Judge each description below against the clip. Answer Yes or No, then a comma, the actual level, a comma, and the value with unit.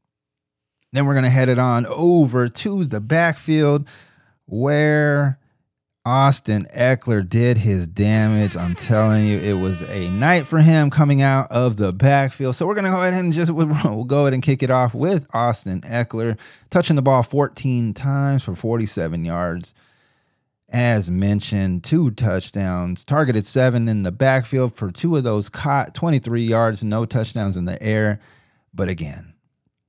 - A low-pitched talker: Yes, low, 125 Hz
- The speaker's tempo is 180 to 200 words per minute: No, average, 155 wpm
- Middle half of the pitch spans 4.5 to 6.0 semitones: Yes, average, 5.0 semitones